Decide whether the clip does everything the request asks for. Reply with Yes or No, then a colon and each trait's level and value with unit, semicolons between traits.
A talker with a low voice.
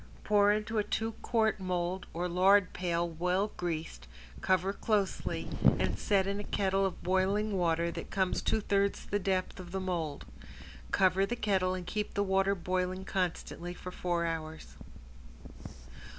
No: medium, 185 Hz